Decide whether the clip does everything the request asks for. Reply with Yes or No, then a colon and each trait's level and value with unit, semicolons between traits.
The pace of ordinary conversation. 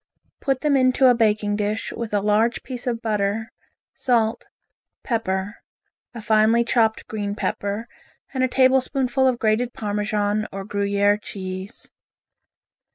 No: slow, 130 wpm